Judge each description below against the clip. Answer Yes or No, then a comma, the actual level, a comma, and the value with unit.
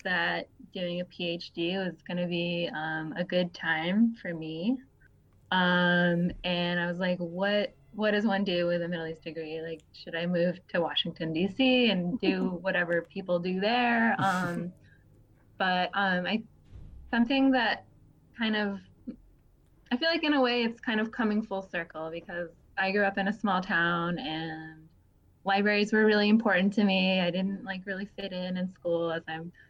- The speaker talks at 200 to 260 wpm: No, average, 175 wpm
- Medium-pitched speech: Yes, medium, 180 Hz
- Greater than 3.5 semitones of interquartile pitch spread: No, average, 3.2 semitones